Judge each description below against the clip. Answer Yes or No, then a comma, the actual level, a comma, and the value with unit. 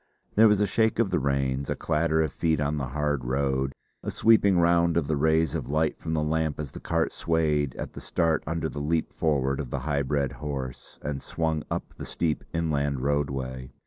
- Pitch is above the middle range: No, very low, 75 Hz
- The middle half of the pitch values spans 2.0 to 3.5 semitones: Yes, average, 2.9 semitones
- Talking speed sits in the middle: No, fast, 210 wpm